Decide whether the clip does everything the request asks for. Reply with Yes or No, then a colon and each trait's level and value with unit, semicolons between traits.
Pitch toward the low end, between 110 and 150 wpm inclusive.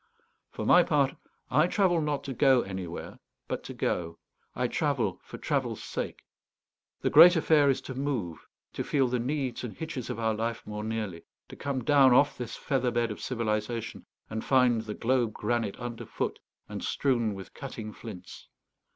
No: low, 120 Hz; average, 170 wpm